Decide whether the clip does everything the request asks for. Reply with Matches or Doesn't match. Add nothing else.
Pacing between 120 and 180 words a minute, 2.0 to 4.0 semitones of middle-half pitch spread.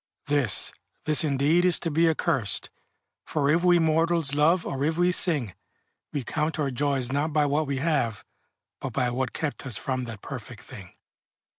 Matches